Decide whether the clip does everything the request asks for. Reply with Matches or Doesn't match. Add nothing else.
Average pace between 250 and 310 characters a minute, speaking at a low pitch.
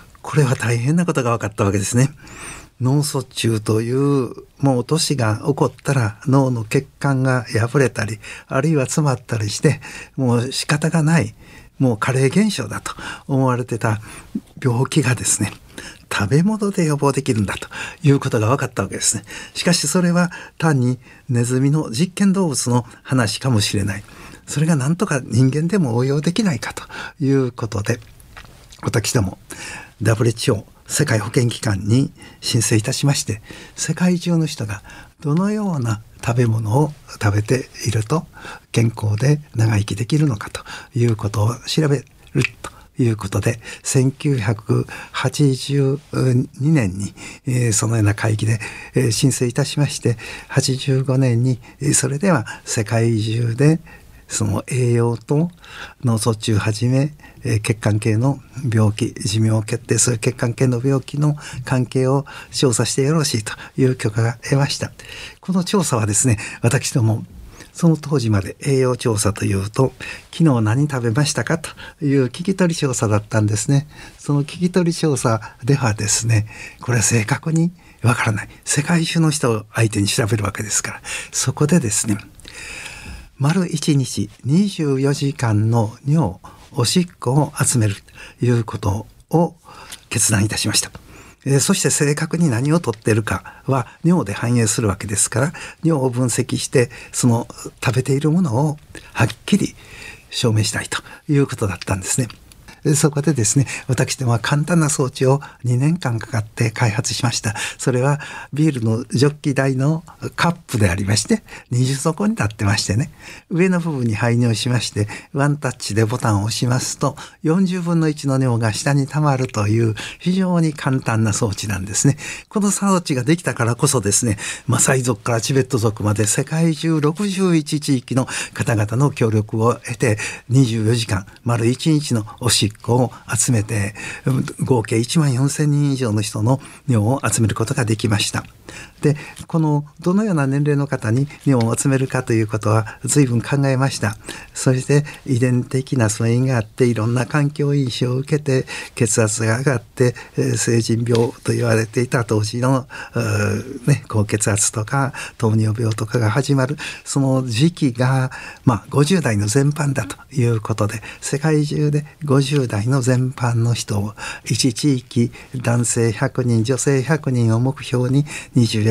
Matches